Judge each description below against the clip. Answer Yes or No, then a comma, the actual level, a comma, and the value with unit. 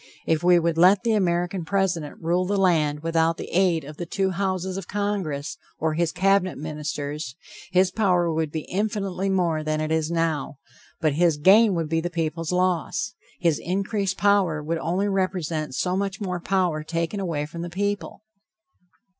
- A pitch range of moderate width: Yes, average, 3.2 semitones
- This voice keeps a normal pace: Yes, average, 175 wpm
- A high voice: No, medium, 175 Hz